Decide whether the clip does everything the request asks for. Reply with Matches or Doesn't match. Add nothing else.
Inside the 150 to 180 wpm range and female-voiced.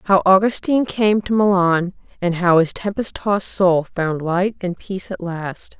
Matches